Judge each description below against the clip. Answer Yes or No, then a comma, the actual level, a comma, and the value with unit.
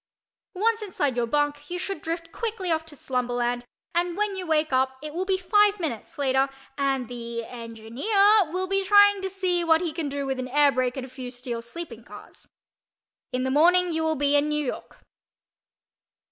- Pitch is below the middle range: No, very high, 300 Hz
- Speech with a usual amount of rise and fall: No, wide, 6.0 semitones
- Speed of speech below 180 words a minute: No, average, 190 wpm